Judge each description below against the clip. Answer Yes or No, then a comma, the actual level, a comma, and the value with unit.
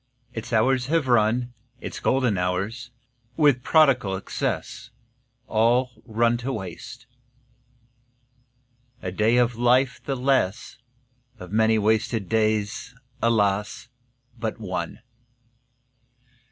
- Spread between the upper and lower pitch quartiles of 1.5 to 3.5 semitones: Yes, average, 2.7 semitones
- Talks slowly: Yes, slow, 100 wpm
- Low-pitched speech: Yes, low, 115 Hz